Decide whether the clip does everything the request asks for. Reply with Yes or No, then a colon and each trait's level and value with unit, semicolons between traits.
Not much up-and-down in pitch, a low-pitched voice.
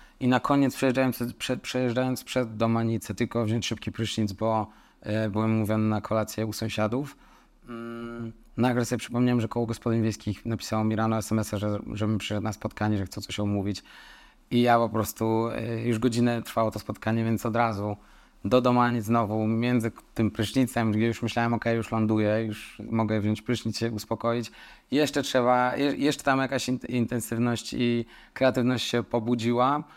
Yes: narrow, 1.9 semitones; low, 115 Hz